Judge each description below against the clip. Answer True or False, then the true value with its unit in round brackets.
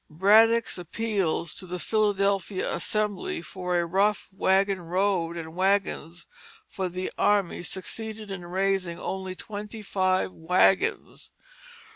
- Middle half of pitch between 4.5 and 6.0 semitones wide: False (2.4 semitones)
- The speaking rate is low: True (115 wpm)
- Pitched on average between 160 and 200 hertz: True (190 Hz)